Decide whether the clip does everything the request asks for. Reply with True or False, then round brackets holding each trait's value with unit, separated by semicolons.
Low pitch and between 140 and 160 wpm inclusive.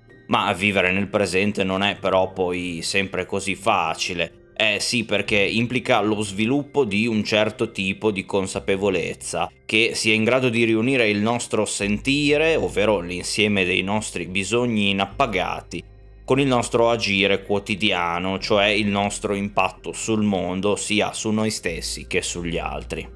True (100 Hz; 145 wpm)